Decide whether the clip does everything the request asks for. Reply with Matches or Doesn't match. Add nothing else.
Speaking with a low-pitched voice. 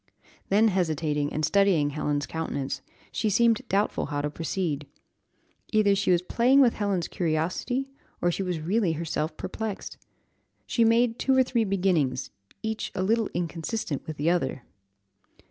Doesn't match